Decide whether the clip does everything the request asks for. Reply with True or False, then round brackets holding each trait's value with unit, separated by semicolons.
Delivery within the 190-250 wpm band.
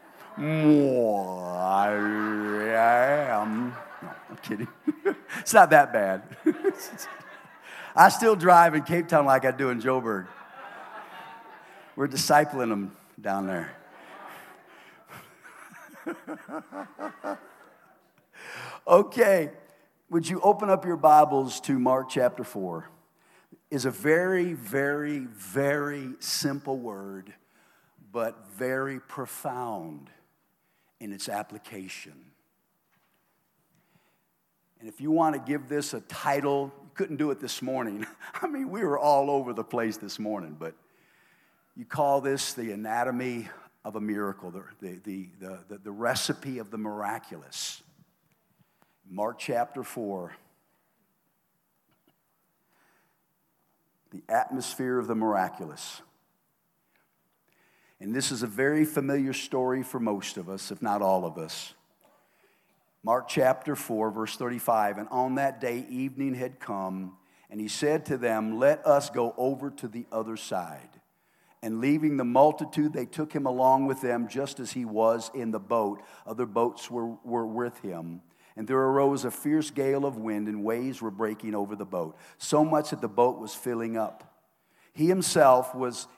False (135 wpm)